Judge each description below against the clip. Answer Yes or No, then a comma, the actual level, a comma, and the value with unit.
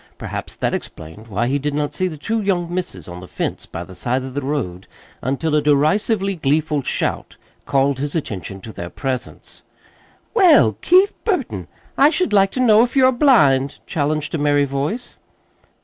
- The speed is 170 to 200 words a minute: Yes, average, 180 wpm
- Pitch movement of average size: No, wide, 7.3 semitones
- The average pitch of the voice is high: No, medium, 145 Hz